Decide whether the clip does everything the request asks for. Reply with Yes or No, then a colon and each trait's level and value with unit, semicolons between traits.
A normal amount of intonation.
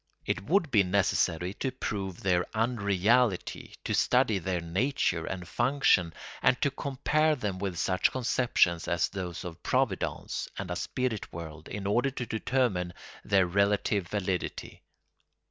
No: wide, 5.8 semitones